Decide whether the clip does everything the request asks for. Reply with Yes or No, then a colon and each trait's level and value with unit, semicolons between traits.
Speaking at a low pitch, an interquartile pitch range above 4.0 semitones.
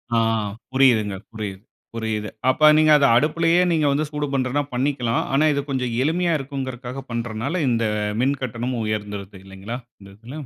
Yes: low, 125 Hz; average, 4.4 semitones